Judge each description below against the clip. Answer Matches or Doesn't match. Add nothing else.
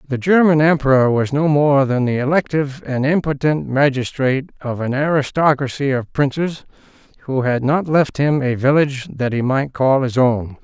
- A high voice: Doesn't match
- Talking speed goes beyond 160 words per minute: Matches